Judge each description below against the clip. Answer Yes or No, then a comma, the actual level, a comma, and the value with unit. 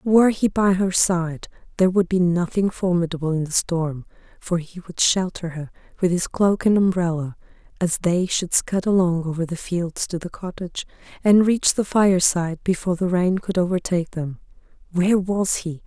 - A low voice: No, medium, 180 Hz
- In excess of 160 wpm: Yes, average, 180 wpm